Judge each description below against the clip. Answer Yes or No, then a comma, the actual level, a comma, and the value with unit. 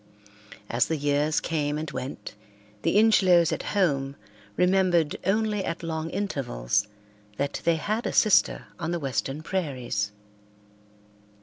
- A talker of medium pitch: Yes, medium, 160 Hz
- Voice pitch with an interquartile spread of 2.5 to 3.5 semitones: No, average, 4.9 semitones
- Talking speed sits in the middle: No, slow, 125 wpm